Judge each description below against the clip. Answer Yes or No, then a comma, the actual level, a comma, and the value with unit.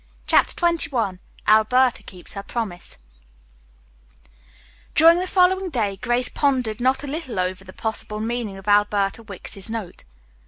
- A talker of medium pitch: No, high, 225 Hz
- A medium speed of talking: No, slow, 130 wpm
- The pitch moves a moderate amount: Yes, average, 4.9 semitones